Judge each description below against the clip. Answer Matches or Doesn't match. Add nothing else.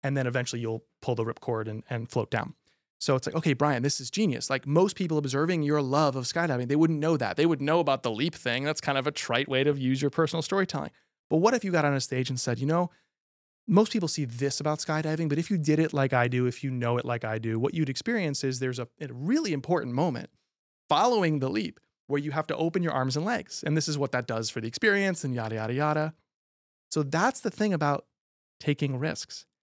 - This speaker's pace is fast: Matches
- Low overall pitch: Doesn't match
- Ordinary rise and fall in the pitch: Matches